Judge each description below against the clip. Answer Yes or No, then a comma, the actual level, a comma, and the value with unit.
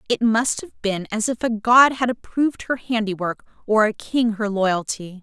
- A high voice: Yes, high, 220 Hz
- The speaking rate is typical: Yes, average, 195 wpm